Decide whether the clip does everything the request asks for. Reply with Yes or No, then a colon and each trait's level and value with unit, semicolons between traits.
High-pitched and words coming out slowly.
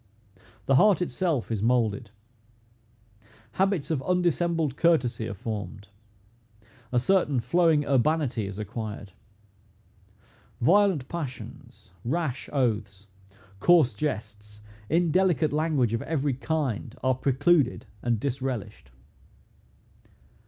No: low, 135 Hz; slow, 95 wpm